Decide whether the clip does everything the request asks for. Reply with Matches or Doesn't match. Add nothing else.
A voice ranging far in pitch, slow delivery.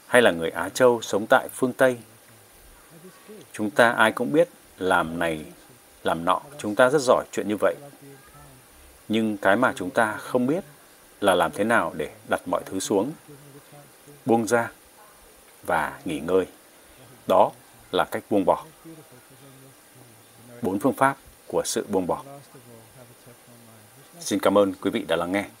Doesn't match